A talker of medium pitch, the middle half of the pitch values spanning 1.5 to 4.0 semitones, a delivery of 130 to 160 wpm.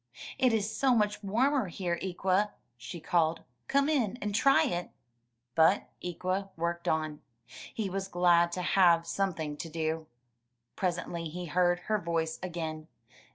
Yes: medium, 180 Hz; average, 3.6 semitones; average, 150 wpm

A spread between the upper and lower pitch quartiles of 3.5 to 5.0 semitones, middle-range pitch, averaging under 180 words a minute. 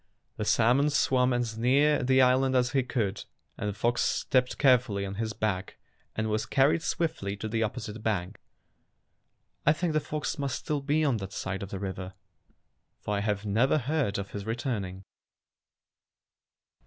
No: average, 4.7 semitones; low, 115 Hz; average, 170 wpm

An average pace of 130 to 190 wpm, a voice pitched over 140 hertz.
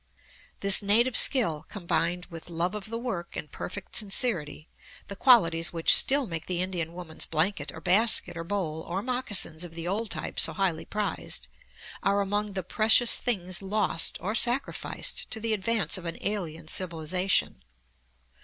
Yes: average, 160 wpm; high, 190 Hz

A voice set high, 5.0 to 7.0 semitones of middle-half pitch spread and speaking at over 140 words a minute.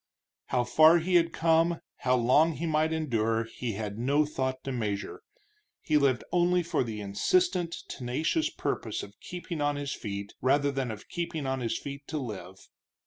No: medium, 140 Hz; average, 5.3 semitones; average, 180 wpm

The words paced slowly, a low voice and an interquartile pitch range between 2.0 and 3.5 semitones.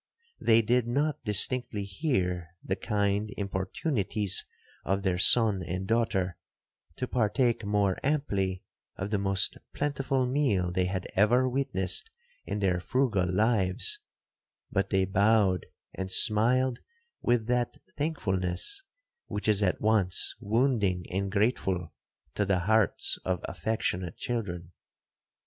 No: slow, 120 wpm; low, 105 Hz; average, 4.3 semitones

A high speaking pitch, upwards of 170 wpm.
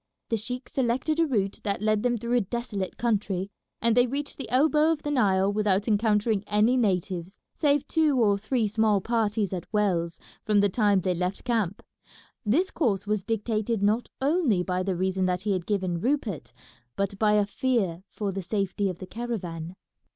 Yes: high, 210 Hz; average, 185 wpm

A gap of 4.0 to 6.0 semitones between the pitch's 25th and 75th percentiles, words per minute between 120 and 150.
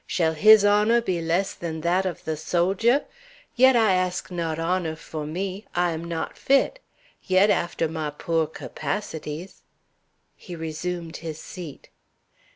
No: average, 3.1 semitones; average, 145 wpm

